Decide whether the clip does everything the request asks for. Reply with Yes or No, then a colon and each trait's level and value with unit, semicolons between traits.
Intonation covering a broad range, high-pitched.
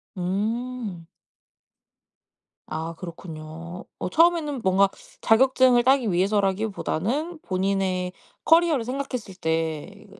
Yes: wide, 5.8 semitones; high, 200 Hz